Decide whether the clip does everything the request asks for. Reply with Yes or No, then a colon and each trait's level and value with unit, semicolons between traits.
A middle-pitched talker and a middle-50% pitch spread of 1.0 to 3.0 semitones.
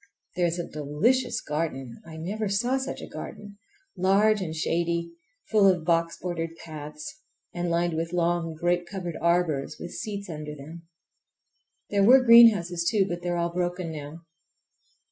No: medium, 175 Hz; average, 3.4 semitones